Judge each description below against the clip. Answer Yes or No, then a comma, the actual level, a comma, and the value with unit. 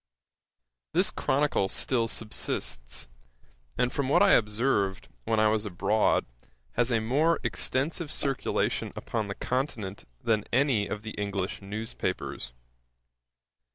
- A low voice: Yes, low, 110 Hz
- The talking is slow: Yes, slow, 120 wpm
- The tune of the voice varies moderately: Yes, average, 4.3 semitones